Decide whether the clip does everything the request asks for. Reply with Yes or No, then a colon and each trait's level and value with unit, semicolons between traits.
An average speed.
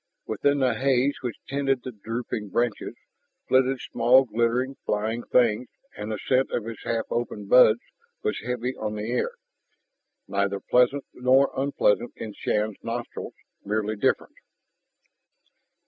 No: slow, 130 wpm